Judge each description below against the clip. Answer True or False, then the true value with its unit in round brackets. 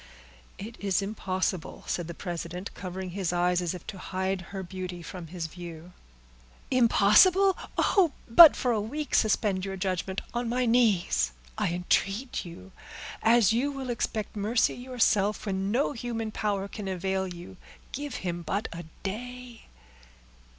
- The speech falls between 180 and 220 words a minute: False (150 wpm)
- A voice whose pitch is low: False (195 Hz)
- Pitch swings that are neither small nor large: True (4.5 semitones)